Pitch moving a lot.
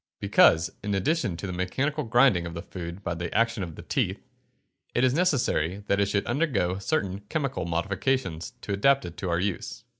Yes: wide, 6.8 semitones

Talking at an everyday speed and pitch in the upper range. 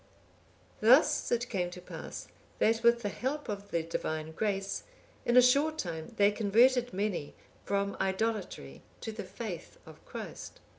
Yes: average, 150 wpm; high, 210 Hz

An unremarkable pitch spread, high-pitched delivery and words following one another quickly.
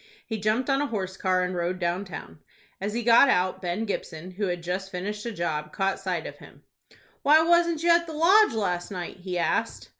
Yes: average, 5.0 semitones; high, 195 Hz; fast, 215 wpm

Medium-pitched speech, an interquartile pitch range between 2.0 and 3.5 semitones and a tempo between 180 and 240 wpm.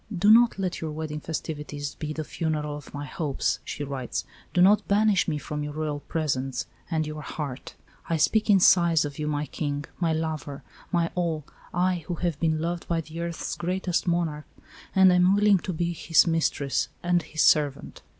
Yes: medium, 160 Hz; average, 2.9 semitones; average, 190 wpm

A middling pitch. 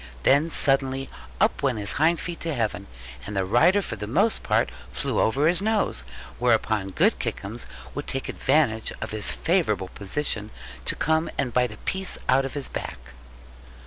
No: low, 130 Hz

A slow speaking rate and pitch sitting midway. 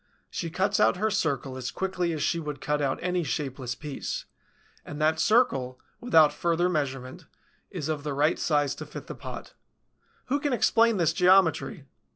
No: average, 175 wpm; medium, 155 Hz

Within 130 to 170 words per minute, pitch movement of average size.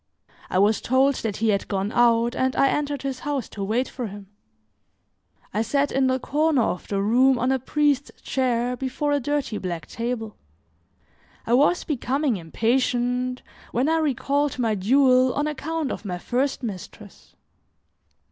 Yes: average, 160 wpm; average, 3.8 semitones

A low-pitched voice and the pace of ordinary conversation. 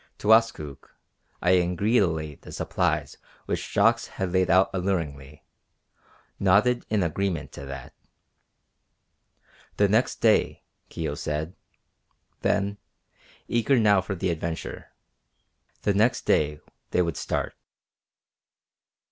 No: very low, 90 Hz; slow, 105 wpm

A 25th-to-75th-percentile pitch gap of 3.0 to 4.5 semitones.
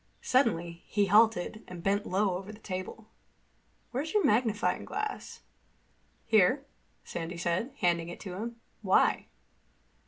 Yes: average, 4.1 semitones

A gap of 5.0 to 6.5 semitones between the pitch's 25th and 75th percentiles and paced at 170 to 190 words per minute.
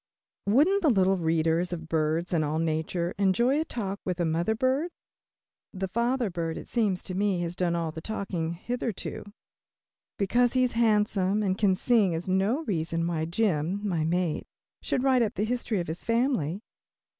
Yes: wide, 5.5 semitones; average, 180 wpm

